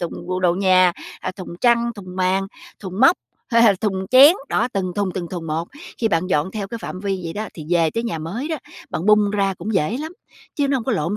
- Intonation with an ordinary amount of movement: Yes, average, 4.0 semitones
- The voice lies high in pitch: Yes, high, 195 Hz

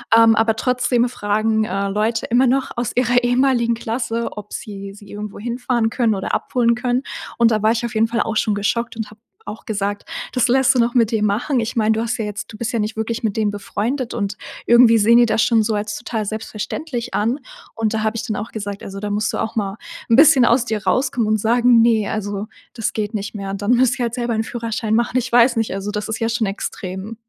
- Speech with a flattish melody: Yes, narrow, 2.2 semitones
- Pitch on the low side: No, high, 225 Hz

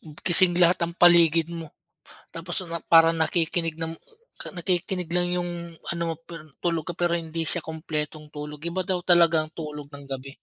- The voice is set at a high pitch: No, medium, 165 Hz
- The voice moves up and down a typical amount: No, narrow, 1.9 semitones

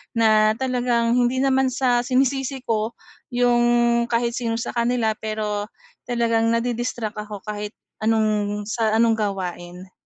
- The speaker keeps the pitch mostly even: Yes, narrow, 2.2 semitones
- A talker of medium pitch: No, high, 230 Hz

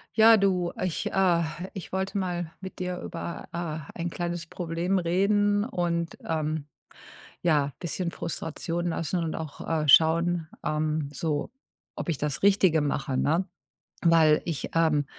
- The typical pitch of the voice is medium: Yes, medium, 170 Hz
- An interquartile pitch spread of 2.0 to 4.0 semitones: Yes, narrow, 2.5 semitones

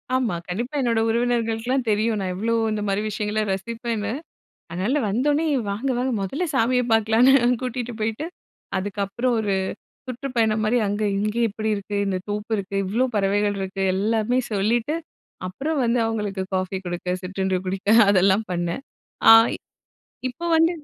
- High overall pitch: Yes, high, 215 Hz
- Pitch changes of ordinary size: Yes, average, 3.6 semitones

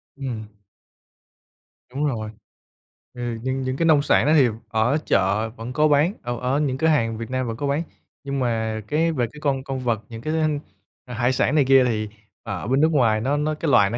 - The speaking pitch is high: No, low, 130 Hz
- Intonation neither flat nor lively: Yes, average, 4.2 semitones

